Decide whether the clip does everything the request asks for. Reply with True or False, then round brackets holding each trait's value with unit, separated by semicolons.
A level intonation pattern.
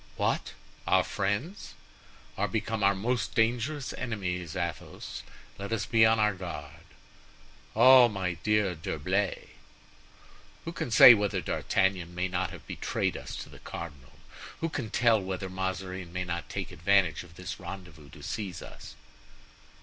False (3.7 semitones)